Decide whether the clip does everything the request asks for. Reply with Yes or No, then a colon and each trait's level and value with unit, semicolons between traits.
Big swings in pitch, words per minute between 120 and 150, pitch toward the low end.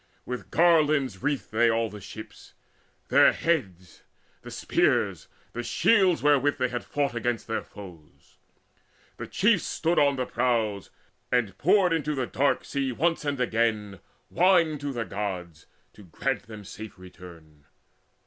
Yes: wide, 6.1 semitones; average, 145 wpm; low, 120 Hz